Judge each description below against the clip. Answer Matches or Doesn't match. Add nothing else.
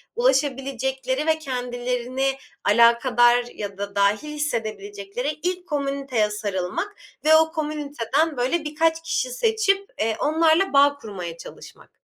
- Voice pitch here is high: Matches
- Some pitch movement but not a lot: Doesn't match